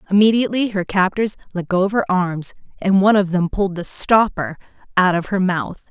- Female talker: Yes, female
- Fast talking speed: No, average, 195 wpm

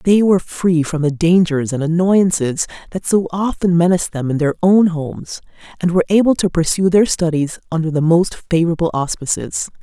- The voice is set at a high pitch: No, medium, 170 Hz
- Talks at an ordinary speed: Yes, average, 175 wpm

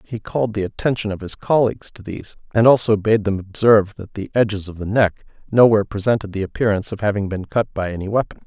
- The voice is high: No, low, 105 Hz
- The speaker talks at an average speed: No, fast, 220 wpm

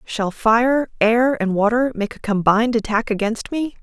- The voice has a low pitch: No, high, 230 Hz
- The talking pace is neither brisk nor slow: Yes, average, 175 wpm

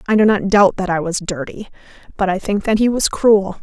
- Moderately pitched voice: No, high, 200 Hz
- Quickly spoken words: Yes, fast, 230 wpm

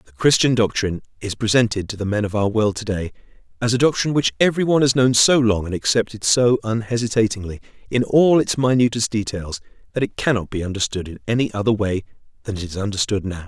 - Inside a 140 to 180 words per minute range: No, average, 200 wpm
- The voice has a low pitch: Yes, low, 110 Hz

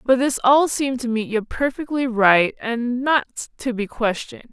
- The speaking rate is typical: Yes, average, 175 wpm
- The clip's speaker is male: No, female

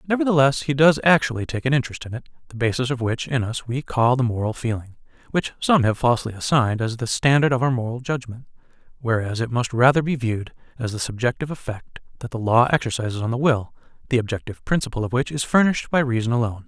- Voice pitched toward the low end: Yes, low, 125 Hz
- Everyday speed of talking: No, fast, 210 wpm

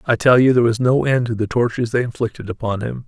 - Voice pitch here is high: No, low, 120 Hz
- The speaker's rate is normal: No, fast, 275 wpm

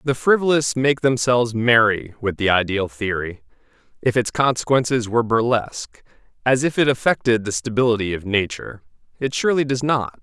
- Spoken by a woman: No, male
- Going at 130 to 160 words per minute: Yes, average, 155 wpm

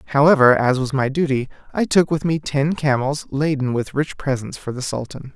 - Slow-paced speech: No, average, 200 wpm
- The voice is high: No, medium, 140 Hz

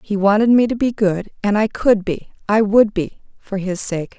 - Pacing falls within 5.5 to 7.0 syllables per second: No, 4.6 syllables/s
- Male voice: No, female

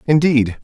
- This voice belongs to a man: Yes, male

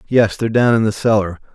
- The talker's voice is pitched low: Yes, low, 110 Hz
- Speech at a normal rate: No, fast, 235 wpm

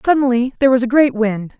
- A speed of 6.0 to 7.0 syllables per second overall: Yes, 6.4 syllables/s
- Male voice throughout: No, female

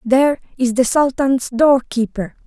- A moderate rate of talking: Yes, average, 145 wpm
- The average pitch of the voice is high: Yes, very high, 255 Hz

